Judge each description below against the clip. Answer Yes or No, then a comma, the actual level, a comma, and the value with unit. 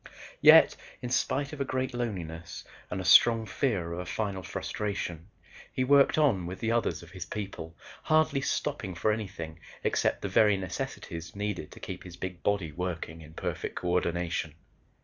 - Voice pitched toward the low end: Yes, very low, 95 Hz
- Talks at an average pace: Yes, average, 170 wpm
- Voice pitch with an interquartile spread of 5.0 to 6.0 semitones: Yes, average, 5.3 semitones